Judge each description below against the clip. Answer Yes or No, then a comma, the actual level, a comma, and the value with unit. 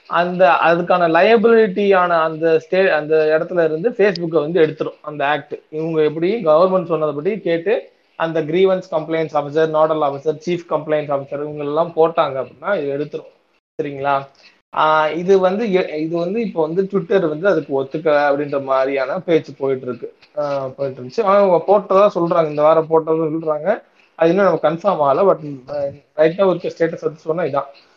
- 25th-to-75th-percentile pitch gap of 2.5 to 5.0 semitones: Yes, average, 3.7 semitones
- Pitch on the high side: No, medium, 160 Hz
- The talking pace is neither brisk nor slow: No, fast, 150 wpm